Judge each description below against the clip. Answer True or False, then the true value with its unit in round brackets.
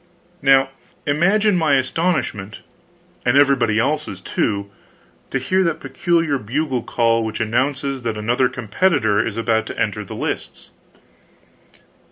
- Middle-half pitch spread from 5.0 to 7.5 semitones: True (5.3 semitones)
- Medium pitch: False (130 Hz)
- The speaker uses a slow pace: True (125 wpm)